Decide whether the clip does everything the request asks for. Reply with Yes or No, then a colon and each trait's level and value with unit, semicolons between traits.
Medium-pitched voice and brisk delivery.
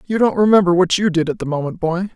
Yes: medium, 180 Hz; fast, 280 wpm